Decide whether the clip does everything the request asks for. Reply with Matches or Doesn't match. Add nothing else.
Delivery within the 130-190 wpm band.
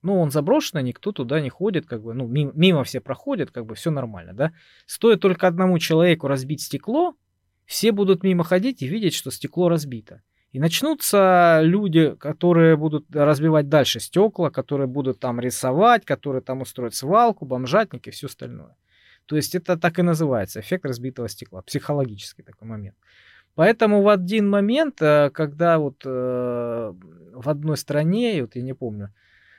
Matches